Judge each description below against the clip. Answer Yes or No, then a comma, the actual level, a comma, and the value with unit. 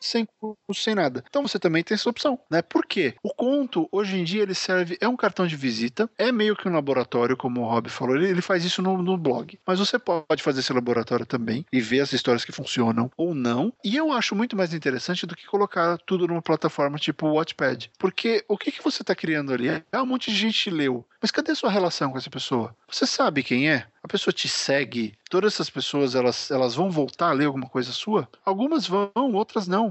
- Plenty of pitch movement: Yes, wide, 7.8 semitones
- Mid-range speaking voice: Yes, medium, 175 Hz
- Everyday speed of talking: No, fast, 235 wpm